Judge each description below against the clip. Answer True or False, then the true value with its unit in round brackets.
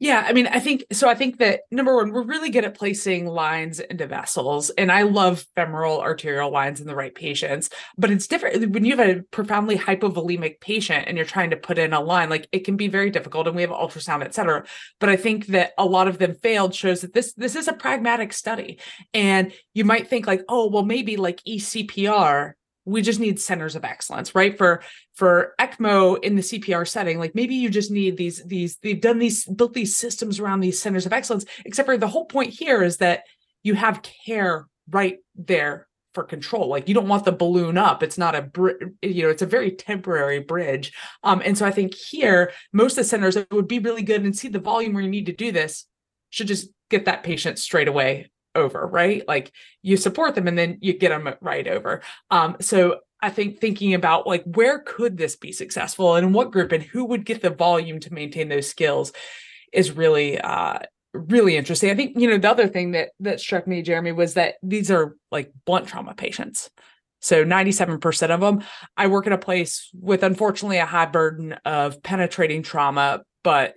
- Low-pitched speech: False (190 Hz)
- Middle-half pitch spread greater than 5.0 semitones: False (3.9 semitones)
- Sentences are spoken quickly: True (215 wpm)